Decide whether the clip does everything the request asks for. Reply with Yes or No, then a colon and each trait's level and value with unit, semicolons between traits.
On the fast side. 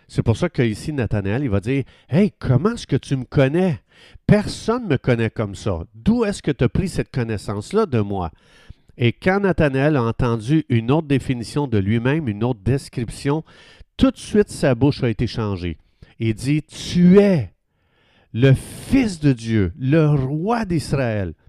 No: average, 180 wpm